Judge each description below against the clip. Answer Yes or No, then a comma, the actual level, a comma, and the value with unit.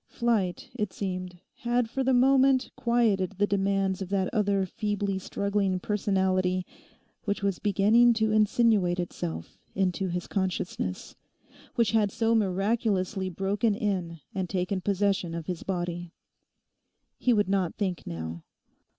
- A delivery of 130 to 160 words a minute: Yes, slow, 135 wpm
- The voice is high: Yes, high, 195 Hz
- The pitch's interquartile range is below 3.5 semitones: Yes, average, 2.7 semitones